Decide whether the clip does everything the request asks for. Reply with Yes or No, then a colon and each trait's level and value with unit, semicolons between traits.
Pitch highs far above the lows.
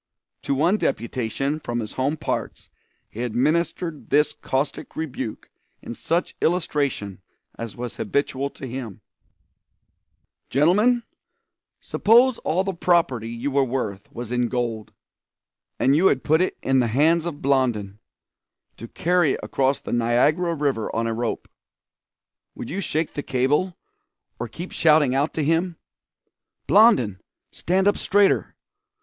Yes: wide, 5.8 semitones